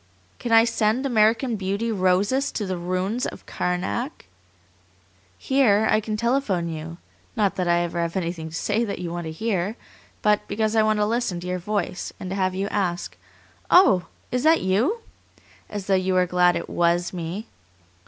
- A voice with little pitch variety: No, average, 3.8 semitones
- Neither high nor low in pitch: No, high, 195 Hz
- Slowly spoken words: No, average, 185 wpm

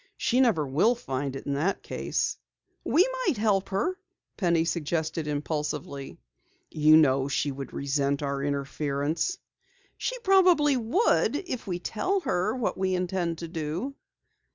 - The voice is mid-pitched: Yes, medium, 170 Hz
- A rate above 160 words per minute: No, average, 140 wpm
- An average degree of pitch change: No, wide, 8.2 semitones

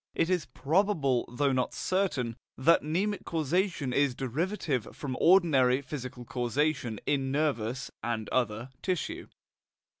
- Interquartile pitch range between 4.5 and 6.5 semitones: Yes, average, 4.9 semitones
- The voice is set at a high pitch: No, medium, 140 Hz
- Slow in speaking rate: Yes, slow, 120 wpm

